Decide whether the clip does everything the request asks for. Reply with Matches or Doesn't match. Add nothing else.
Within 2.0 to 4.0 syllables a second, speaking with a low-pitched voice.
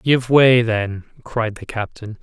Matches